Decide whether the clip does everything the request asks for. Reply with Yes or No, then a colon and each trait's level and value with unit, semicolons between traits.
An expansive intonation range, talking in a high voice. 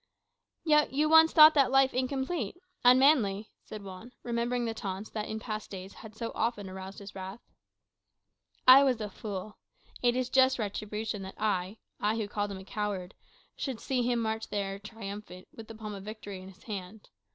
No: average, 3.9 semitones; high, 215 Hz